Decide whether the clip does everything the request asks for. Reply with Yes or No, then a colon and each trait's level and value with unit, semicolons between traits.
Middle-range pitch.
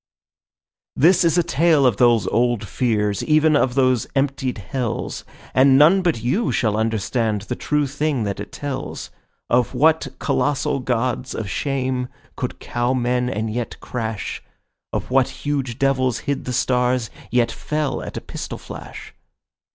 No: low, 130 Hz